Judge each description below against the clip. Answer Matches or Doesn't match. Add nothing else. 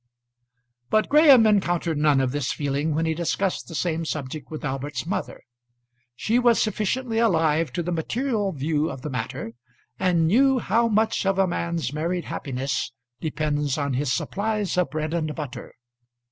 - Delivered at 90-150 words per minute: Doesn't match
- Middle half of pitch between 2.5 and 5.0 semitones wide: Doesn't match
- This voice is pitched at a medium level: Matches